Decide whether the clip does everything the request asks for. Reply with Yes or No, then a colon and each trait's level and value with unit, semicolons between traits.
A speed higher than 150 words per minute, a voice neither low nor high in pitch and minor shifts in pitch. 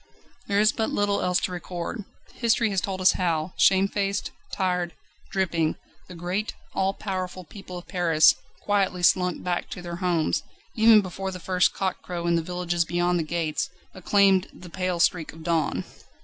Yes: average, 170 wpm; medium, 180 Hz; narrow, 2.0 semitones